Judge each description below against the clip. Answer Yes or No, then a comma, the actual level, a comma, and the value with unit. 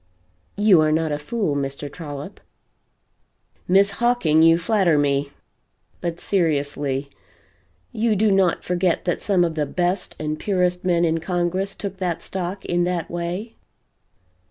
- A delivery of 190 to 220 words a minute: No, average, 140 wpm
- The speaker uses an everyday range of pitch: Yes, average, 3.7 semitones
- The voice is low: No, medium, 175 Hz